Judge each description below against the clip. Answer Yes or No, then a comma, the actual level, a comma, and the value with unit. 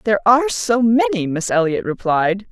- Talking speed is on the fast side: No, average, 165 wpm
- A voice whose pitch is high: Yes, high, 195 Hz